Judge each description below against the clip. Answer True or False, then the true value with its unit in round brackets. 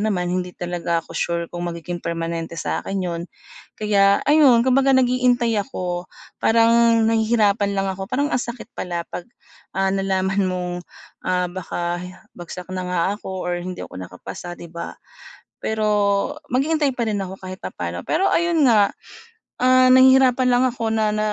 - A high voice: True (200 Hz)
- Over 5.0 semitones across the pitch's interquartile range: True (5.4 semitones)